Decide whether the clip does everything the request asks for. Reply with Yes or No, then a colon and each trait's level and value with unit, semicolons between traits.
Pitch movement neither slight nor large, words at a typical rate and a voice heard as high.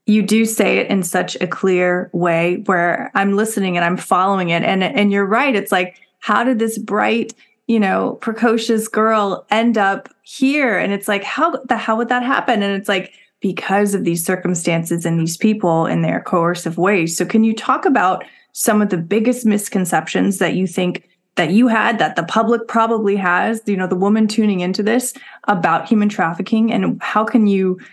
Yes: average, 3.7 semitones; average, 195 wpm; high, 205 Hz